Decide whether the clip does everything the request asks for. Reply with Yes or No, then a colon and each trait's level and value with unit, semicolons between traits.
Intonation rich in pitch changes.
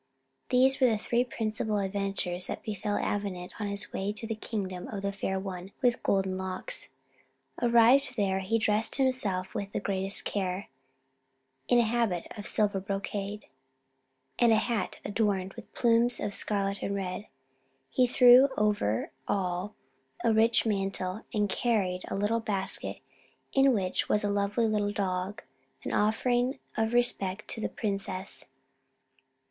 No: average, 2.9 semitones